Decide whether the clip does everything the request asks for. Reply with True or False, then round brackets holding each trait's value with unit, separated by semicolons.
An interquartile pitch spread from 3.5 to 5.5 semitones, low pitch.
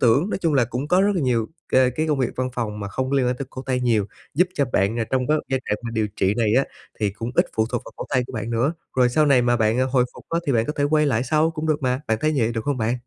True (3.9 semitones; 125 Hz)